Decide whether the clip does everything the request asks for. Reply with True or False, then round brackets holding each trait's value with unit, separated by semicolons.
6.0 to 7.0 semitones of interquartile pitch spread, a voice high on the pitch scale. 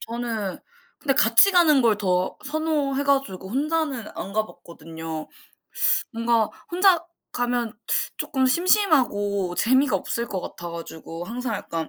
True (6.6 semitones; 235 Hz)